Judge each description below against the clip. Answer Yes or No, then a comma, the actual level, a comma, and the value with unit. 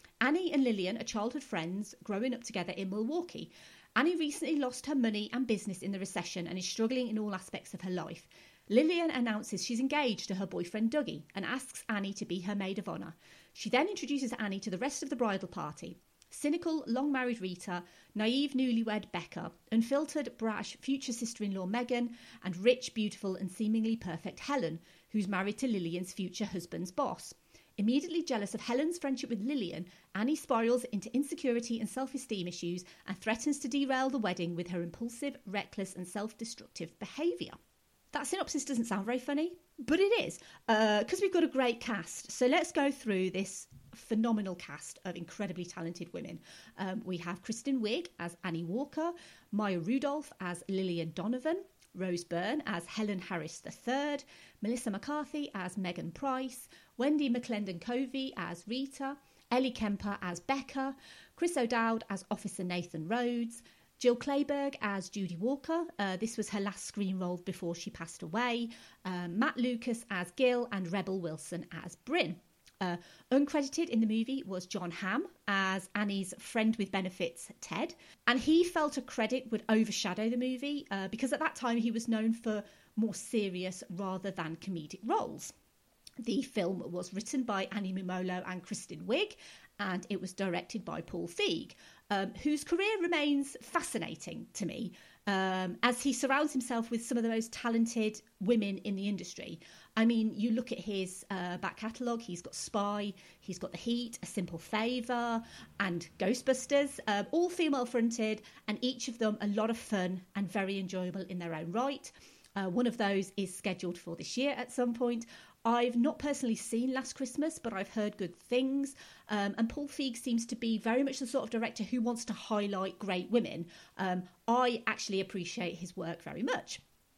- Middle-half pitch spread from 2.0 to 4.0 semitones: No, average, 5.2 semitones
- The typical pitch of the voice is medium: No, high, 220 Hz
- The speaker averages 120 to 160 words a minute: No, average, 175 wpm